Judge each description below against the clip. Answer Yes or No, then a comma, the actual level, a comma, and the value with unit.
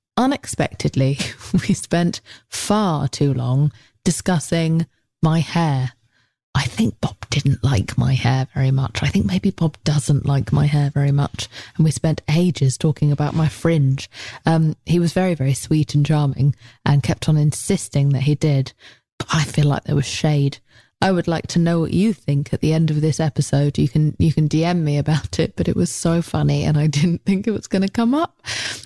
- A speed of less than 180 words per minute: No, average, 200 wpm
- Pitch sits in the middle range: Yes, medium, 150 Hz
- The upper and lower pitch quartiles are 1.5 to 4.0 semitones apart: Yes, average, 3.3 semitones